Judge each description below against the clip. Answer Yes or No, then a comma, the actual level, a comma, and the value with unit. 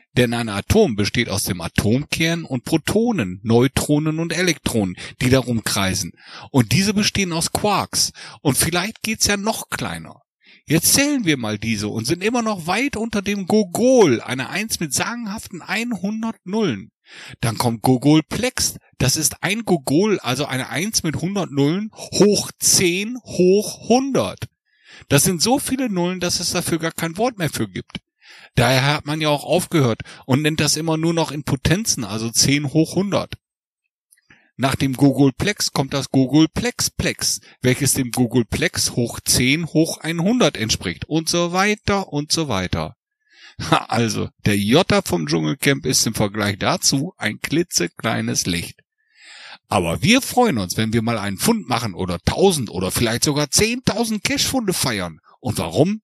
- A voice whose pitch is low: No, medium, 155 Hz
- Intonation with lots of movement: Yes, wide, 8.3 semitones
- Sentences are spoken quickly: No, average, 155 wpm